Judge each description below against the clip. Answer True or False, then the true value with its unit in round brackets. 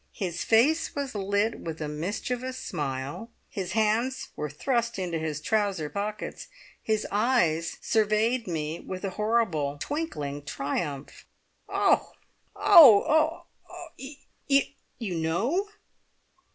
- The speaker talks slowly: True (110 wpm)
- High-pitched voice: True (205 Hz)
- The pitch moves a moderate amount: False (6.8 semitones)